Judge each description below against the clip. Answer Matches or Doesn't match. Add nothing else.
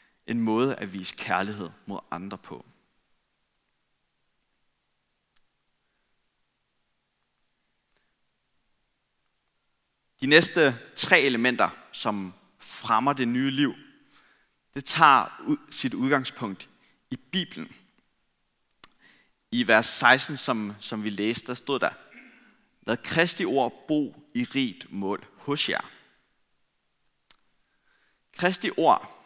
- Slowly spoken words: Matches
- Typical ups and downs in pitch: Doesn't match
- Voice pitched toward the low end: Matches